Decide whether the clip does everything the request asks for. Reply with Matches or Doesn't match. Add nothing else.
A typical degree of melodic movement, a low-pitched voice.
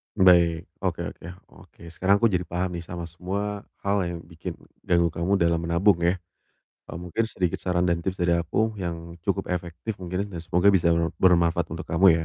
Doesn't match